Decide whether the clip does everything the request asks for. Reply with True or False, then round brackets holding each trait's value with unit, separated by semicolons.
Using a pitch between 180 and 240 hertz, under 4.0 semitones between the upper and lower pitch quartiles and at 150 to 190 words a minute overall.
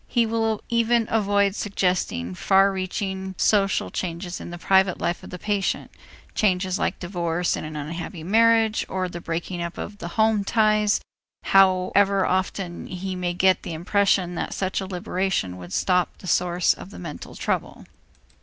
True (190 Hz; 2.5 semitones; 160 wpm)